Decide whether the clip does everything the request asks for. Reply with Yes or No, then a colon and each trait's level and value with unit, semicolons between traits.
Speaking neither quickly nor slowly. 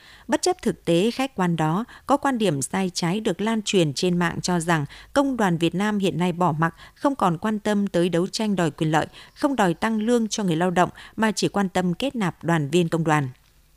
Yes: average, 240 wpm